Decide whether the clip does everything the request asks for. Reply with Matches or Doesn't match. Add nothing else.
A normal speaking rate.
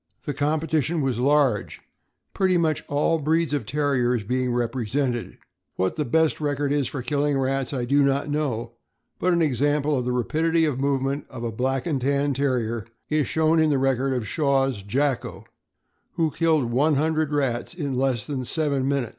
Matches